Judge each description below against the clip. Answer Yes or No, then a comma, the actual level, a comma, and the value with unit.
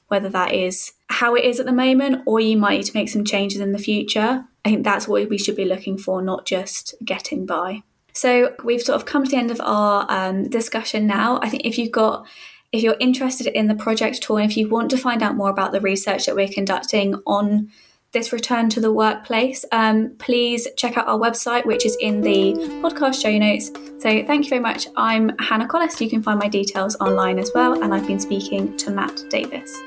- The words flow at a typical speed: No, fast, 225 wpm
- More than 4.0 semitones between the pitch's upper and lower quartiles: No, average, 3.5 semitones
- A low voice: No, high, 220 Hz